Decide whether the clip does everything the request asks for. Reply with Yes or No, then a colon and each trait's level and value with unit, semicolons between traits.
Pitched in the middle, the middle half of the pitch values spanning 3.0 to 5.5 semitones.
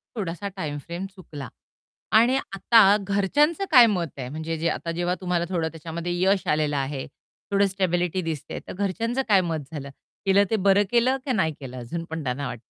Yes: medium, 175 Hz; average, 4.1 semitones